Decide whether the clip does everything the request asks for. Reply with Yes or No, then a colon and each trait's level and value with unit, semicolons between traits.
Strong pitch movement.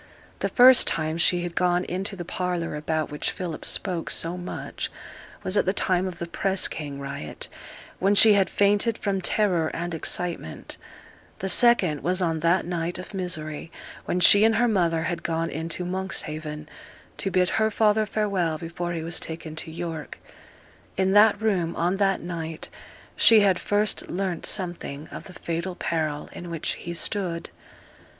No: average, 2.9 semitones